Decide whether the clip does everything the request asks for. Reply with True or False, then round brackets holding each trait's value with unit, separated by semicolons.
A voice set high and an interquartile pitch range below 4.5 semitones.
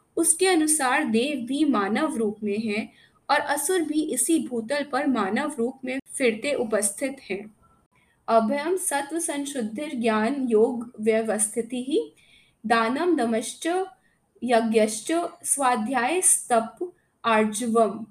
False (250 Hz; 4.8 semitones)